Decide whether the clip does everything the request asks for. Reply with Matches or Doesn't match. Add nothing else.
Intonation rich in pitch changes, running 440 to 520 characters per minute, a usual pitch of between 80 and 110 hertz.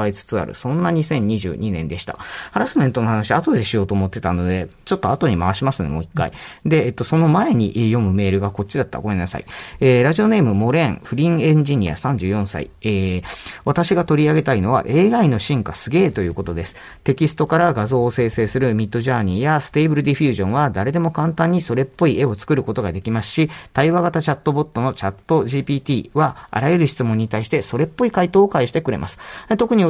Doesn't match